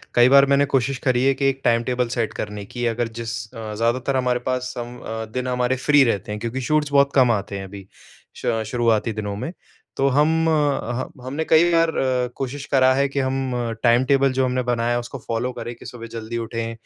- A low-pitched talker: Yes, low, 125 Hz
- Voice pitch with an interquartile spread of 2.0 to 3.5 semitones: Yes, average, 2.7 semitones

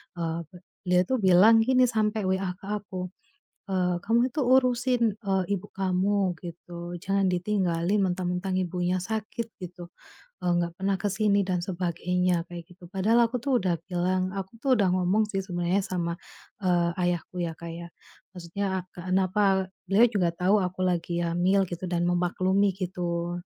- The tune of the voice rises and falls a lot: No, narrow, 2.4 semitones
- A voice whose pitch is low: No, medium, 185 Hz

